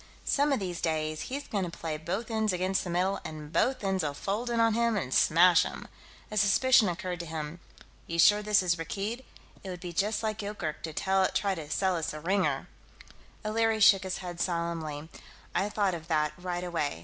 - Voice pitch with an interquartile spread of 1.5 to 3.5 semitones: No, average, 4.0 semitones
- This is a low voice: No, medium, 185 Hz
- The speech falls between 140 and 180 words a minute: No, average, 200 wpm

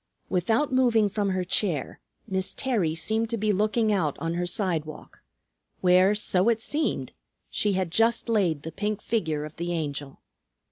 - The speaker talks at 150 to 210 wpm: Yes, average, 160 wpm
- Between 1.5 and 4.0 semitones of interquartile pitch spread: No, average, 4.5 semitones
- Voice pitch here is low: No, high, 190 Hz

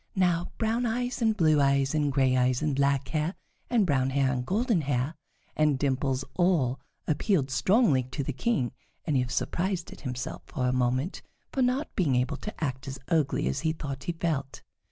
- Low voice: No, medium, 145 Hz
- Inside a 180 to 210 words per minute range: Yes, average, 195 wpm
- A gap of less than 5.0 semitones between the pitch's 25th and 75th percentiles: No, average, 5.3 semitones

